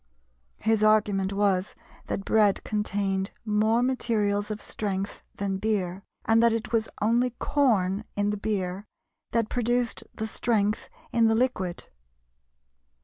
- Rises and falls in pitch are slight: Yes, narrow, 2.3 semitones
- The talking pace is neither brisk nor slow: No, slow, 130 wpm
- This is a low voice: No, high, 210 Hz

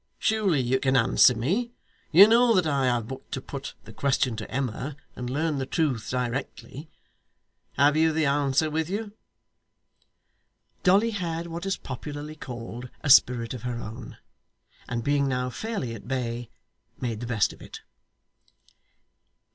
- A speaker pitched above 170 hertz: No, low, 135 Hz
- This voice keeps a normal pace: Yes, average, 155 wpm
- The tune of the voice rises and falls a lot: No, average, 4.6 semitones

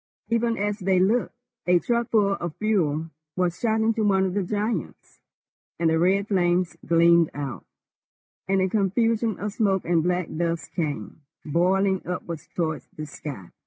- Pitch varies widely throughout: No, average, 3.7 semitones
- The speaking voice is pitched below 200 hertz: Yes, medium, 185 Hz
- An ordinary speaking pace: Yes, average, 155 wpm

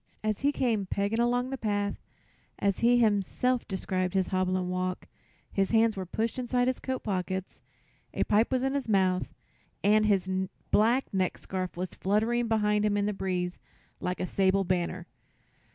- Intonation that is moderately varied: Yes, average, 3.8 semitones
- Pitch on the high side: Yes, high, 205 Hz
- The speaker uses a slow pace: No, average, 165 wpm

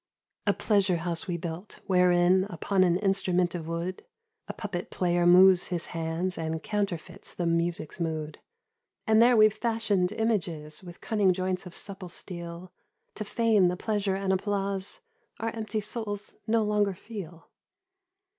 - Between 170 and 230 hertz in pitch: Yes, medium, 185 Hz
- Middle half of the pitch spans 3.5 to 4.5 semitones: No, average, 3.1 semitones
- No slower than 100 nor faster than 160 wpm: Yes, average, 150 wpm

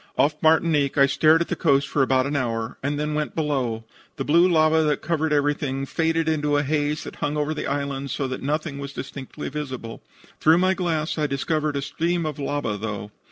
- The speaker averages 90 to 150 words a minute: No, fast, 205 wpm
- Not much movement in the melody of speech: Yes, narrow, 2.3 semitones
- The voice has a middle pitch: Yes, medium, 145 Hz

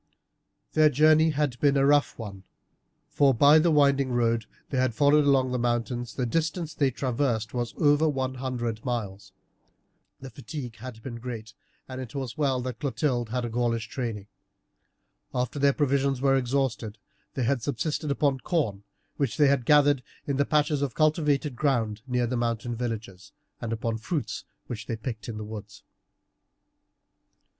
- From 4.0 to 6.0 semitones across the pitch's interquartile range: No, average, 3.5 semitones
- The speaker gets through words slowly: No, average, 165 wpm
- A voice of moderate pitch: No, low, 130 Hz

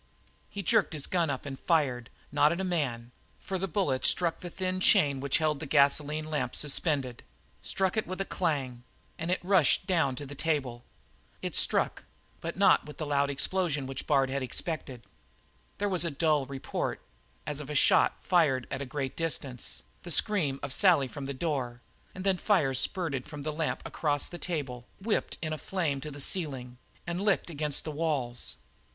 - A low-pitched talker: No, medium, 150 Hz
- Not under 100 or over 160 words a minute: No, average, 190 wpm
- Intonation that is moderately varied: Yes, average, 4.2 semitones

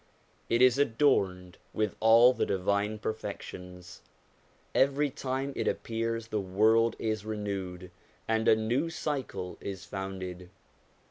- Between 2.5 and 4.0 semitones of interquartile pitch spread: Yes, average, 3.6 semitones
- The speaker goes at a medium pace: No, slow, 120 wpm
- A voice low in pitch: Yes, low, 110 Hz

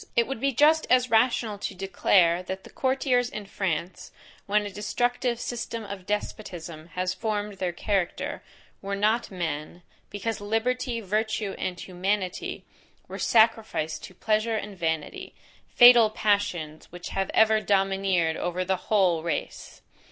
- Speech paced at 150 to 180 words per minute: No, average, 140 wpm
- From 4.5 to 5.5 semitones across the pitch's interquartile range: No, average, 3.6 semitones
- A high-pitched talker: Yes, high, 205 Hz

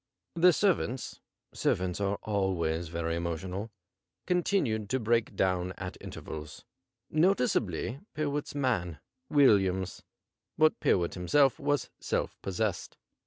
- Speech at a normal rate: No, slow, 110 wpm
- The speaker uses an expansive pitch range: Yes, wide, 7.9 semitones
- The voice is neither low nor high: No, low, 100 Hz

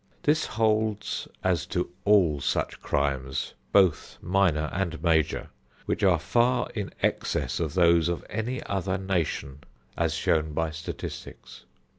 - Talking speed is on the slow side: Yes, slow, 130 wpm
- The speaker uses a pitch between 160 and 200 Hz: No, very low, 90 Hz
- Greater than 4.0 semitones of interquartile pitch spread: Yes, average, 4.5 semitones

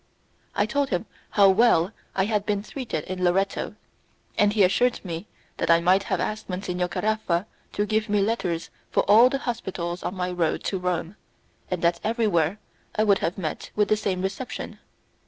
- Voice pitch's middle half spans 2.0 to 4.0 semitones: Yes, average, 3.1 semitones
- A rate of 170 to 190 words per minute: Yes, average, 180 wpm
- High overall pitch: Yes, high, 195 Hz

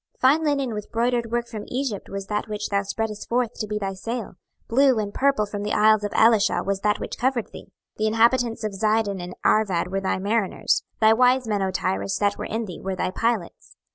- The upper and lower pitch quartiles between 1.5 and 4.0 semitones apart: Yes, average, 2.8 semitones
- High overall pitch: Yes, high, 215 Hz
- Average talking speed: No, fast, 230 wpm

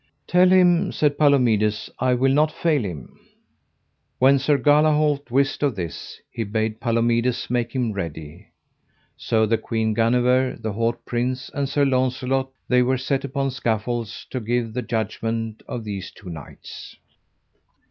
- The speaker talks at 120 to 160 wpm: Yes, average, 145 wpm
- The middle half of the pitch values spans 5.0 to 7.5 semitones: No, average, 3.5 semitones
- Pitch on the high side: No, low, 125 Hz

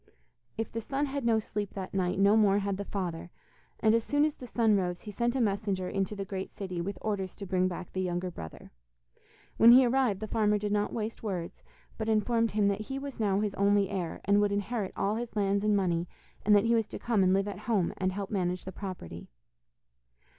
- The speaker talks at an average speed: No, fast, 230 wpm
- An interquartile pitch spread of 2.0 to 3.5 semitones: Yes, average, 2.8 semitones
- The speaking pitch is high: Yes, high, 205 Hz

